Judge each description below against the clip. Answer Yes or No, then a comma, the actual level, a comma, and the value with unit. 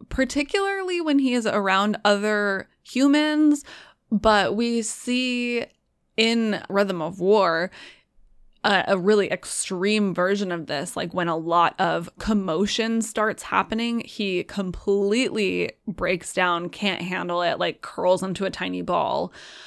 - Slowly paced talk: Yes, slow, 130 wpm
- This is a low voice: No, high, 205 Hz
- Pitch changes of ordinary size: Yes, average, 4.1 semitones